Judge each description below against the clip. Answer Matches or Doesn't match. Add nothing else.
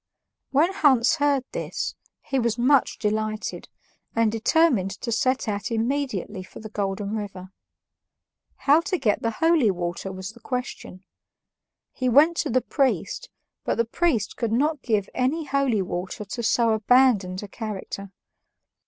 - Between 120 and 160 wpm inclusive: Matches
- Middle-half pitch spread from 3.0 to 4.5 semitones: Doesn't match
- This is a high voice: Matches